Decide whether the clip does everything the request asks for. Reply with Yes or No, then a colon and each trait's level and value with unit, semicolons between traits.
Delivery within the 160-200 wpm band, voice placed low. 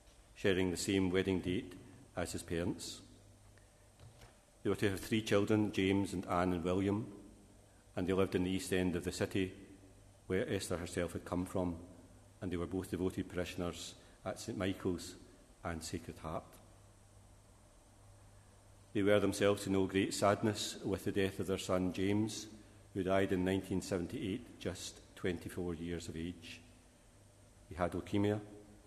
No: average, 150 wpm; very low, 95 Hz